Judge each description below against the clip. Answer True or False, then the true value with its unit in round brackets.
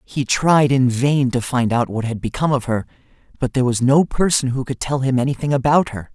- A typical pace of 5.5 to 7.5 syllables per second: True (5.6 syllables/s)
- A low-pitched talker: True (130 Hz)